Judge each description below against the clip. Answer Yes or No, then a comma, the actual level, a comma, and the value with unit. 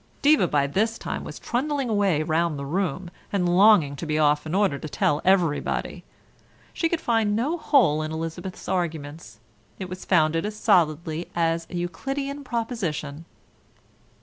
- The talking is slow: No, average, 155 wpm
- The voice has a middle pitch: Yes, medium, 175 Hz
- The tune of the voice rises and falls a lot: Yes, wide, 5.7 semitones